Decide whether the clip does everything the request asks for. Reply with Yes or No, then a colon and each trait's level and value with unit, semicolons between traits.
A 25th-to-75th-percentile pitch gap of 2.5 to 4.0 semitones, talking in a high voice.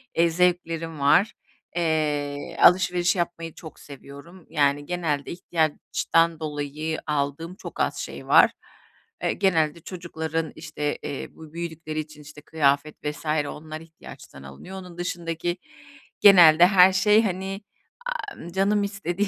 No: average, 2.9 semitones; medium, 165 Hz